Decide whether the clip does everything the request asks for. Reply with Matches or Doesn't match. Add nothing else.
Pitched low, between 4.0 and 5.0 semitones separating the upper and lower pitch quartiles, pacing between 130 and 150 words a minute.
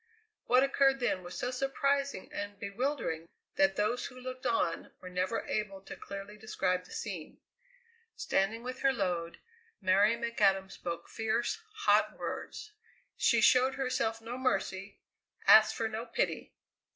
Doesn't match